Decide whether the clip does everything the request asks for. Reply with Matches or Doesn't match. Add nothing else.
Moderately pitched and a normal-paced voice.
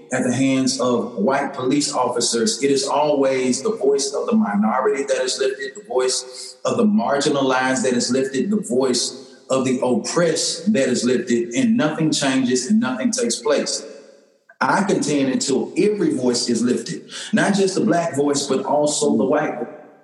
Matches